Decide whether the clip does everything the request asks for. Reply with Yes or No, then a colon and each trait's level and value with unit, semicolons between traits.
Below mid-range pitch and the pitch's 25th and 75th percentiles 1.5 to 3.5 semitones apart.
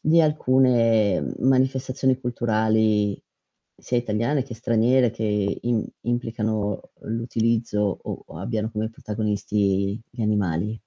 Yes: low, 110 Hz; narrow, 2.6 semitones